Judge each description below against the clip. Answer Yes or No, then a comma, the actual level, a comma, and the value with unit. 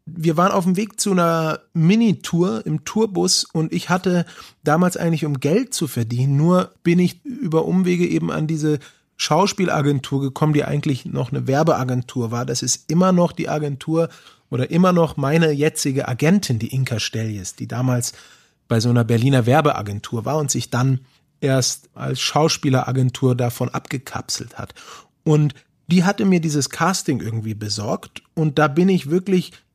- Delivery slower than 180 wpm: Yes, average, 160 wpm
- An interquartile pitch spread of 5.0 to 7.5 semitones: Yes, average, 5.3 semitones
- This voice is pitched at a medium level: Yes, medium, 150 Hz